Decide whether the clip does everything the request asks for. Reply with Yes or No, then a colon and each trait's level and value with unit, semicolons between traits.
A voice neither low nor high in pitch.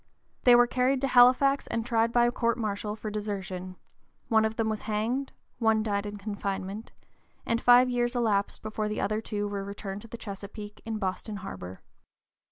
No: high, 215 Hz